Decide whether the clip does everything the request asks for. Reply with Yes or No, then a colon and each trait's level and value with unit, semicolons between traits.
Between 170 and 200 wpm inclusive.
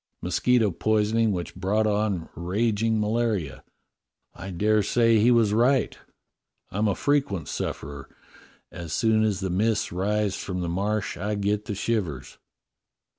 No: average, 140 wpm